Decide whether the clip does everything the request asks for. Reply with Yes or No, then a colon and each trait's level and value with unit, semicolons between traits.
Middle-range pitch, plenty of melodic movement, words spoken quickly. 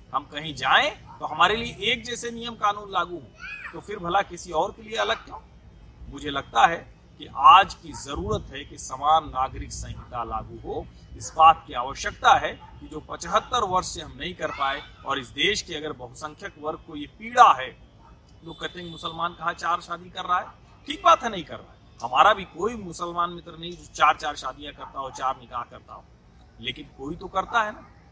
No: medium, 155 Hz; average, 4.9 semitones; fast, 205 wpm